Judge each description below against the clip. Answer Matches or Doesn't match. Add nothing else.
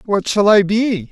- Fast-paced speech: Matches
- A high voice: Matches